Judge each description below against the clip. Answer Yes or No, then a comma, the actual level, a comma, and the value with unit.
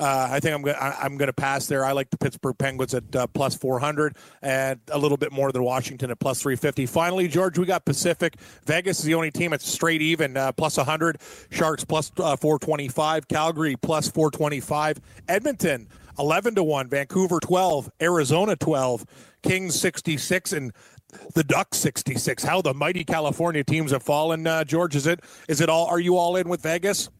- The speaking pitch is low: No, medium, 155 Hz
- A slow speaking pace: No, average, 190 wpm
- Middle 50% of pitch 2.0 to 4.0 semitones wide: Yes, average, 3.3 semitones